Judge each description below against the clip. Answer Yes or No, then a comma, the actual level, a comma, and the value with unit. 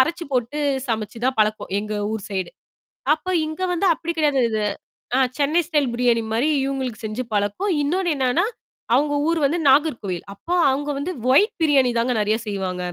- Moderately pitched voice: No, very high, 260 Hz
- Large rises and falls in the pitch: Yes, wide, 6.0 semitones